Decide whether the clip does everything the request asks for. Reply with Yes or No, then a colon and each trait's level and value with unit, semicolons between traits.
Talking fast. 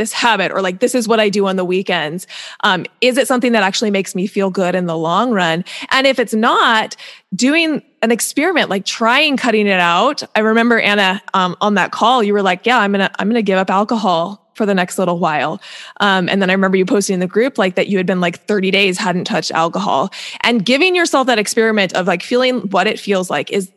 Yes: fast, 240 wpm